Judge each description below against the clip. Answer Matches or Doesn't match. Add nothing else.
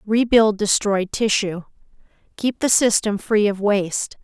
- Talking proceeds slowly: Matches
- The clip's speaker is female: Matches